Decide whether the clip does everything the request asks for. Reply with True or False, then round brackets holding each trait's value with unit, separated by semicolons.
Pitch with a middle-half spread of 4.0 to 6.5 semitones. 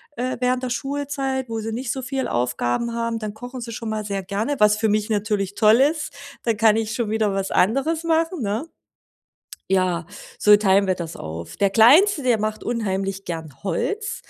True (4.4 semitones)